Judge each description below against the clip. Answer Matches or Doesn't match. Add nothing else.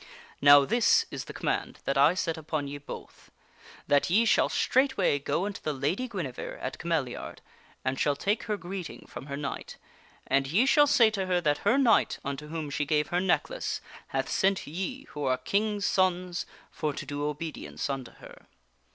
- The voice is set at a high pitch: Doesn't match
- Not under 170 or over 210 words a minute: Matches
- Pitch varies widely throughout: Matches